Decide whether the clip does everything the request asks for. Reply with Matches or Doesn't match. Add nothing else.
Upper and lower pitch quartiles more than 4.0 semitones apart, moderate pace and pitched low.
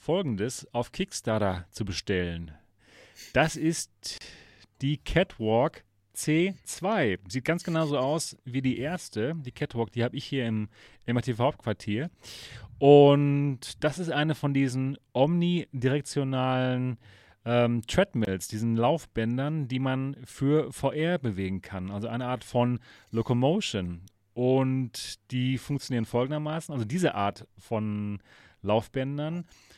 Doesn't match